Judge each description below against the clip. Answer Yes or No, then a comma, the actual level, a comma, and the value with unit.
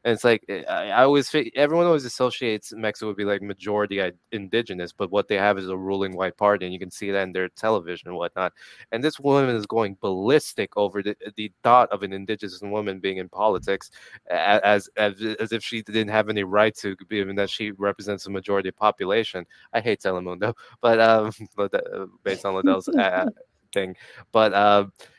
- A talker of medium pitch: No, low, 105 Hz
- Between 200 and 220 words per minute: Yes, fast, 205 wpm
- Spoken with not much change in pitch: Yes, narrow, 2.2 semitones